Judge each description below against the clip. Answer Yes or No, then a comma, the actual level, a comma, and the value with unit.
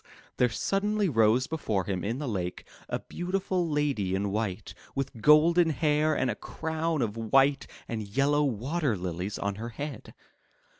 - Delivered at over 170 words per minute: No, average, 160 wpm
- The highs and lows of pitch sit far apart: Yes, wide, 6.5 semitones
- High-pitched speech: No, low, 135 Hz